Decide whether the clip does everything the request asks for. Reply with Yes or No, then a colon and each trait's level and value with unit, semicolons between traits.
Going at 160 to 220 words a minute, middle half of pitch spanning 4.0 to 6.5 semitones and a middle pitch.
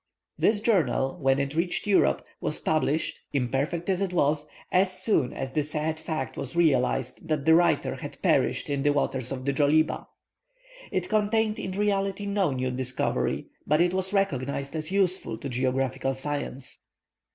Yes: average, 165 wpm; wide, 5.6 semitones; medium, 155 Hz